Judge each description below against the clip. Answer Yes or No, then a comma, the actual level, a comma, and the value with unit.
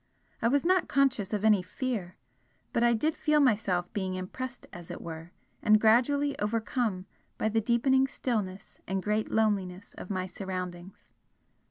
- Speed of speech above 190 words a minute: No, average, 155 wpm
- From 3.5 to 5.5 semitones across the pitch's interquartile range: Yes, average, 5.0 semitones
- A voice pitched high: Yes, high, 215 Hz